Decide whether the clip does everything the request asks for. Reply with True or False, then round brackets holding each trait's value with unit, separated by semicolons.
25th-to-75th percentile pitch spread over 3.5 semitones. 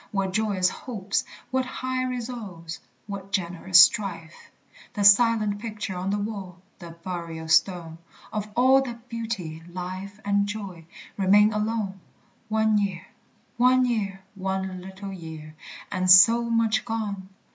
False (3.1 semitones)